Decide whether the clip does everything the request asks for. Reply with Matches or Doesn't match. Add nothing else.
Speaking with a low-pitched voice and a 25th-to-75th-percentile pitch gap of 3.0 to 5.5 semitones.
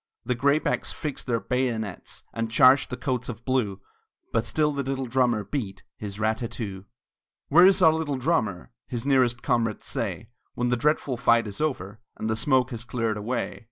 Matches